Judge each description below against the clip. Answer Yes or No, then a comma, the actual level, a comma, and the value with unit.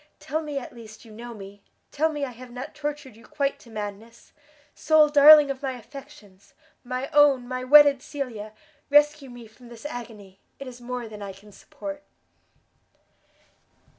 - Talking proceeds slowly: No, average, 165 wpm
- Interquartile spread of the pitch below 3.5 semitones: No, average, 4.5 semitones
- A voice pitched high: Yes, very high, 255 Hz